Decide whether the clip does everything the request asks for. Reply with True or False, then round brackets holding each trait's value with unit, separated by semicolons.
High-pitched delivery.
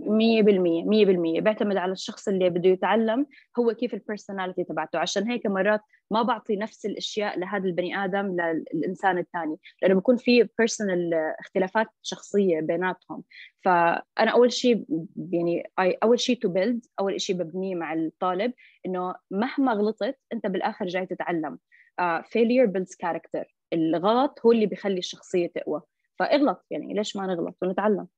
True (195 Hz)